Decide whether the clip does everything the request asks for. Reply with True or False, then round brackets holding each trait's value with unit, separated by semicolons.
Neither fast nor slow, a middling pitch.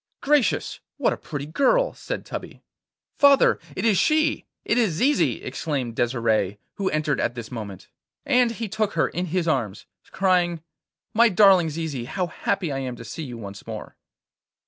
True (170 wpm; 165 Hz)